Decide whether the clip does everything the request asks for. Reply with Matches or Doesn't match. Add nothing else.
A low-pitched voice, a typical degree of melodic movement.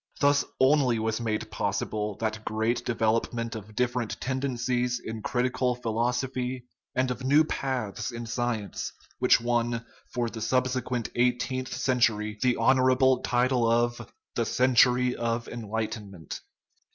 Doesn't match